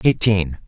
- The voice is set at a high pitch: No, very low, 95 Hz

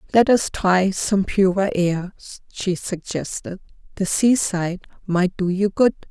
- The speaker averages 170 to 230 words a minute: No, average, 140 wpm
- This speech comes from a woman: Yes, female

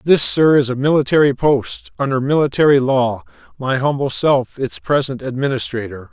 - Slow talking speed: Yes, slow, 125 wpm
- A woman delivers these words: No, male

